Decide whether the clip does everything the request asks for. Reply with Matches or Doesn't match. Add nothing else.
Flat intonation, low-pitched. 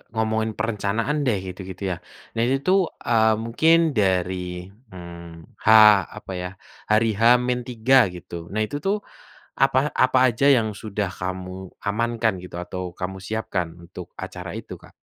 Doesn't match